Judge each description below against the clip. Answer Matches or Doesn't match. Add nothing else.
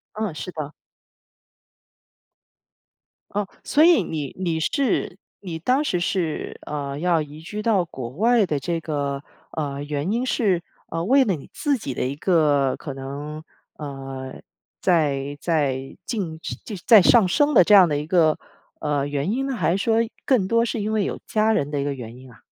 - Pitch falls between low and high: Matches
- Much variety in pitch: Matches